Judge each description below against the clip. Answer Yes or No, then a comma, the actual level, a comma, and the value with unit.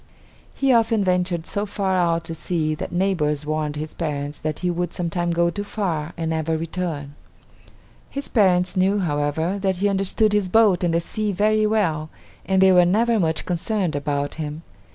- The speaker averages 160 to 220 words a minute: Yes, average, 180 wpm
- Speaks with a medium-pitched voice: Yes, medium, 175 Hz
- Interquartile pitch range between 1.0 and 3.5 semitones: No, average, 3.9 semitones